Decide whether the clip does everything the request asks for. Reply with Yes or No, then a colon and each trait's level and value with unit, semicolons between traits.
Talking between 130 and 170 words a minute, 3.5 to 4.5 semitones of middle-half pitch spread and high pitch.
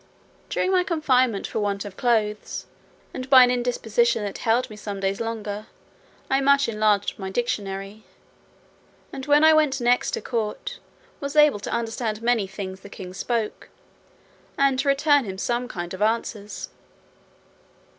Yes: average, 155 wpm; average, 4.2 semitones; high, 230 Hz